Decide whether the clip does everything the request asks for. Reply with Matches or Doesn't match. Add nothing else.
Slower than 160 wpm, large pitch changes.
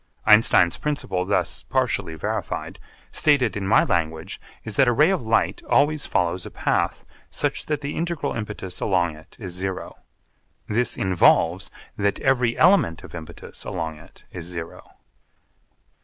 Matches